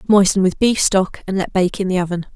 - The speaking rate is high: Yes, fast, 255 wpm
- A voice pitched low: No, high, 190 Hz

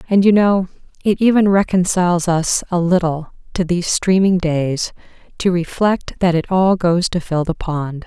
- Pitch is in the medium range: Yes, medium, 180 Hz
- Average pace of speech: Yes, average, 170 wpm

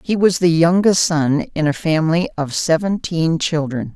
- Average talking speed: Yes, average, 165 wpm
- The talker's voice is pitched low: No, medium, 165 Hz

